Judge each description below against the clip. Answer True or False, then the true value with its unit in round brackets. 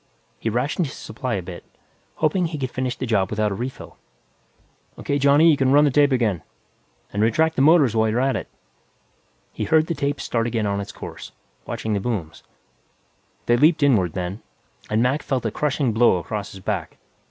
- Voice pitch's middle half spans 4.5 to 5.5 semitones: True (5.2 semitones)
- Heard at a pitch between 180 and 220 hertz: False (125 Hz)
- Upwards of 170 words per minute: True (195 wpm)